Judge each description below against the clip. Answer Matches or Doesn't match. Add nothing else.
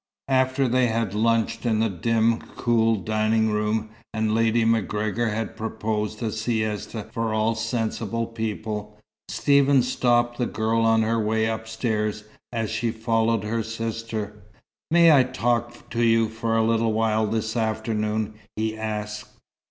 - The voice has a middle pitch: Doesn't match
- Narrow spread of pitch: Matches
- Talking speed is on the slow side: Doesn't match